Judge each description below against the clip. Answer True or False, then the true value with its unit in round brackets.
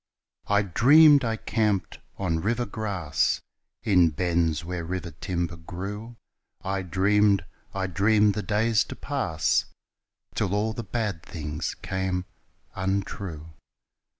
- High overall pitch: False (95 Hz)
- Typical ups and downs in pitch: True (3.6 semitones)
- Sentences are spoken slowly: True (120 wpm)